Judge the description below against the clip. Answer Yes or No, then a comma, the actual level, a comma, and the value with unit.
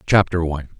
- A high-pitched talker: No, very low, 85 Hz